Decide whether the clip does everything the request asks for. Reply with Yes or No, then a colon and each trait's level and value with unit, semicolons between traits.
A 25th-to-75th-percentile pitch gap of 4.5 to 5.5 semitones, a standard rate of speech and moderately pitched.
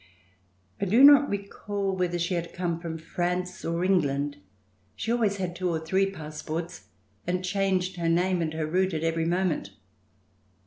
No: narrow, 2.5 semitones; average, 165 wpm; medium, 180 Hz